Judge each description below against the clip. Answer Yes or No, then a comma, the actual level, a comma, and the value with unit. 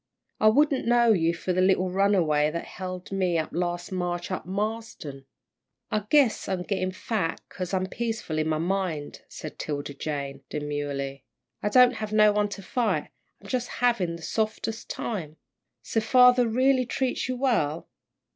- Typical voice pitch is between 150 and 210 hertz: Yes, high, 190 Hz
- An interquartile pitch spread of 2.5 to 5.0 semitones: No, wide, 5.5 semitones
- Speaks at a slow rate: No, average, 165 wpm